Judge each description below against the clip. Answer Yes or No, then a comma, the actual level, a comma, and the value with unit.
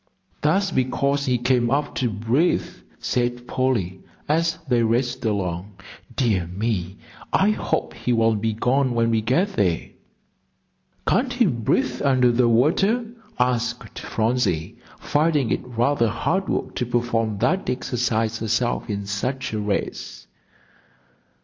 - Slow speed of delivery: Yes, slow, 130 wpm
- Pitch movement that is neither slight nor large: Yes, average, 3.4 semitones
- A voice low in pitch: Yes, low, 120 Hz